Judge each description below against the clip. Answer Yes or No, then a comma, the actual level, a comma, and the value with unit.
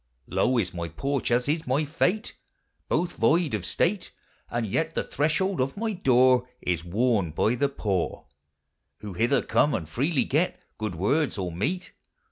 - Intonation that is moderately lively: No, wide, 7.3 semitones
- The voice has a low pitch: Yes, low, 130 Hz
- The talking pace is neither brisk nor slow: Yes, average, 165 wpm